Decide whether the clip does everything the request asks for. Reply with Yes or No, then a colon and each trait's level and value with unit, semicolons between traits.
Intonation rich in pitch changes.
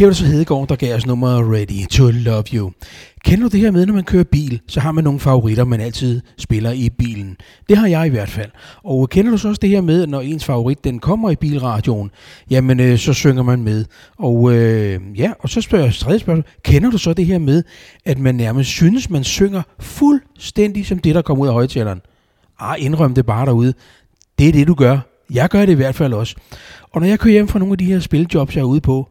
Yes: wide, 6.4 semitones